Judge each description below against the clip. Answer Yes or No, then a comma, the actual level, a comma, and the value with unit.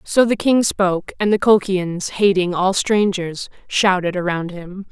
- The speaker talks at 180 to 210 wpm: No, average, 160 wpm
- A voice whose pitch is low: No, high, 190 Hz